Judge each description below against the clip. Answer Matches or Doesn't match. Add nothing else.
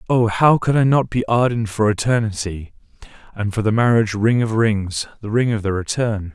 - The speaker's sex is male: Matches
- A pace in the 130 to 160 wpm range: Doesn't match